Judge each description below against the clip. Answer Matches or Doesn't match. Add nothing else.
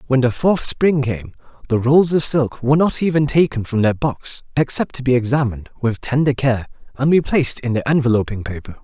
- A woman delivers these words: Doesn't match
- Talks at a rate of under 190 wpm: Doesn't match